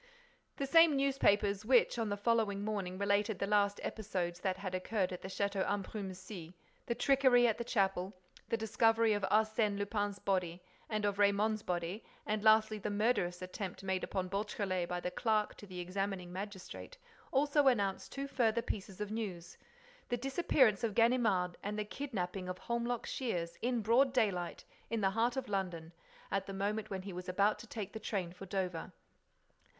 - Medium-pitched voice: No, high, 205 Hz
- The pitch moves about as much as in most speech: Yes, average, 3.2 semitones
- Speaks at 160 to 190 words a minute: Yes, average, 170 wpm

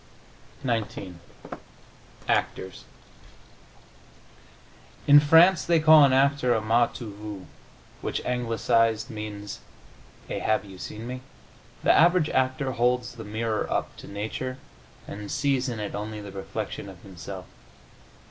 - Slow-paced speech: Yes, slow, 125 wpm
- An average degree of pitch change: Yes, average, 4.0 semitones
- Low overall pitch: Yes, low, 115 Hz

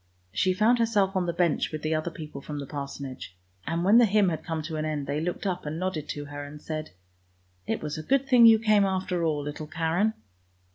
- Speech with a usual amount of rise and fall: Yes, average, 4.3 semitones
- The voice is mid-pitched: Yes, medium, 165 Hz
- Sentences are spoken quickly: Yes, fast, 240 wpm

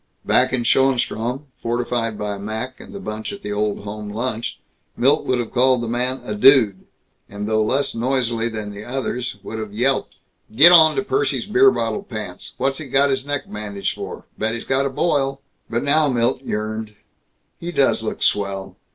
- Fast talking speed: No, average, 185 wpm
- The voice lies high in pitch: No, low, 120 Hz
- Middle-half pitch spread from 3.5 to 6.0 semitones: Yes, average, 4.0 semitones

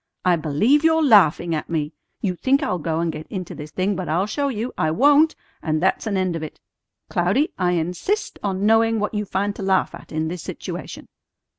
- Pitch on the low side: No, medium, 185 Hz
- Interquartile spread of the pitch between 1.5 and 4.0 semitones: No, average, 5.2 semitones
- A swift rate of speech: Yes, fast, 210 wpm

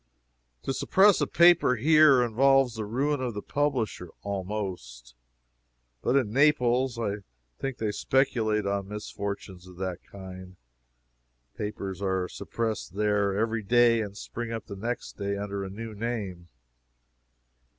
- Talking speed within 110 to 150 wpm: Yes, slow, 135 wpm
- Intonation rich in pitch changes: No, average, 3.8 semitones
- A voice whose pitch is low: Yes, low, 105 Hz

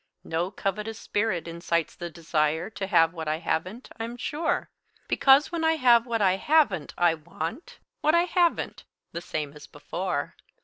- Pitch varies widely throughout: Yes, wide, 7.0 semitones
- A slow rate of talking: No, average, 165 wpm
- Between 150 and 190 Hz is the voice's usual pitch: Yes, medium, 185 Hz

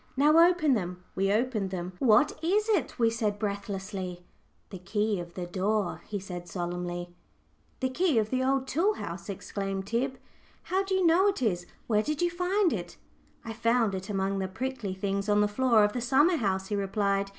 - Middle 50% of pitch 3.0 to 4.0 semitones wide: No, wide, 5.6 semitones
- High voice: Yes, high, 210 Hz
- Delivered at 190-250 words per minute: Yes, average, 195 wpm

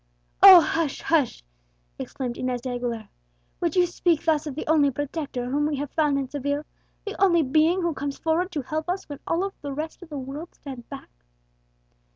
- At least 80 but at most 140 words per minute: No, average, 190 wpm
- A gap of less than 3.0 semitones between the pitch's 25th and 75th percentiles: No, average, 3.4 semitones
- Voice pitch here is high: Yes, very high, 295 Hz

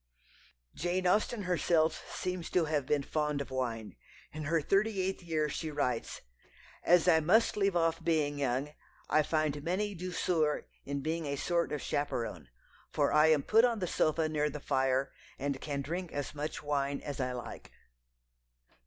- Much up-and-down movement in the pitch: No, average, 3.6 semitones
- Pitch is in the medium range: Yes, medium, 155 Hz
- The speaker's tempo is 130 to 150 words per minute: No, average, 170 wpm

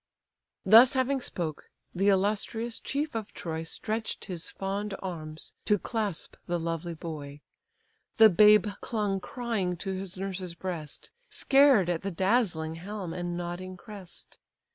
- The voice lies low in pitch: No, high, 190 Hz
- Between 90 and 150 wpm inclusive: Yes, slow, 135 wpm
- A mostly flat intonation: No, average, 3.8 semitones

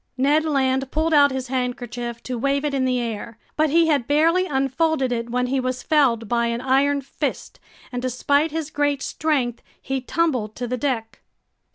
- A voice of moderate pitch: No, very high, 265 Hz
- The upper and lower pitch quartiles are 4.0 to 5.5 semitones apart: No, average, 3.0 semitones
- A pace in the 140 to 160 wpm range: No, average, 185 wpm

